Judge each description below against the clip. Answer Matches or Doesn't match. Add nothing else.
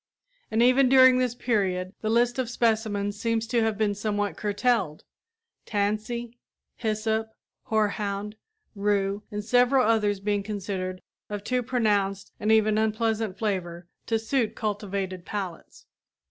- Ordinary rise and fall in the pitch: Doesn't match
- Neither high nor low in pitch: Doesn't match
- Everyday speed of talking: Doesn't match